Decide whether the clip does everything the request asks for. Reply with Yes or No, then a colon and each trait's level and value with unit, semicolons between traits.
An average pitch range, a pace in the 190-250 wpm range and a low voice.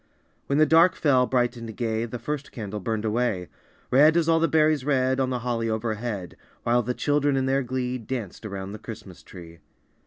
Yes: average, 3.9 semitones; average, 195 wpm; low, 125 Hz